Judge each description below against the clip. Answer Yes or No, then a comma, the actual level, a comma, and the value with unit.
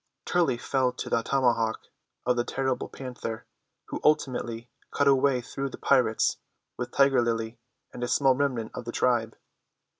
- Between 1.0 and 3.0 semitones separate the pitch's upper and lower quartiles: Yes, narrow, 2.5 semitones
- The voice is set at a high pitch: No, low, 125 Hz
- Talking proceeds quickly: No, average, 160 wpm